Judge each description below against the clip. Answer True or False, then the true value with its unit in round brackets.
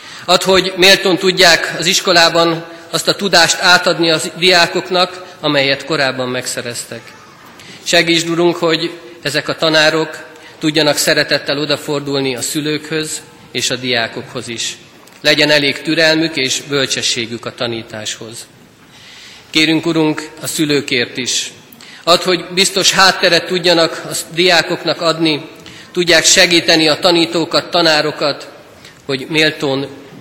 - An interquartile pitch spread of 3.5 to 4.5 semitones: False (2.9 semitones)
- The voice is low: False (160 Hz)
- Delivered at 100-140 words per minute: True (115 wpm)